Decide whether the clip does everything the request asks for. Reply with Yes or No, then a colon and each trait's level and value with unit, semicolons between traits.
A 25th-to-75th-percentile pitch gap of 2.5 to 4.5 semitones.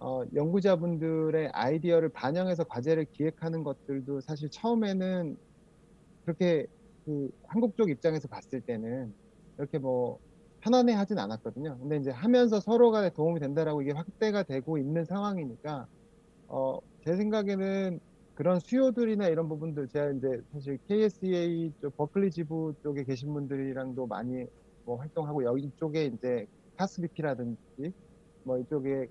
No: average, 5.3 semitones